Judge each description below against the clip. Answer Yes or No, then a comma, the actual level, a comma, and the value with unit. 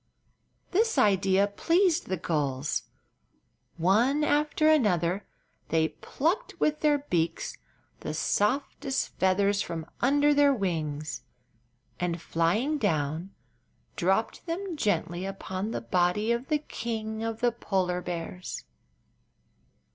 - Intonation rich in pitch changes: Yes, wide, 8.6 semitones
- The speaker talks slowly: Yes, slow, 110 wpm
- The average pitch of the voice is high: Yes, high, 205 Hz